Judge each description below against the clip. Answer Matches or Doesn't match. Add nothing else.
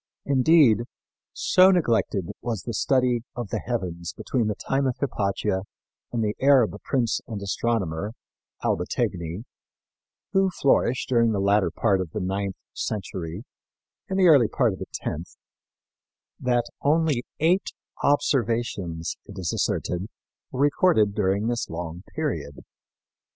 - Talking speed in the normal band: Doesn't match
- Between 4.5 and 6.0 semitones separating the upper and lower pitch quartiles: Matches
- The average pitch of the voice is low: Matches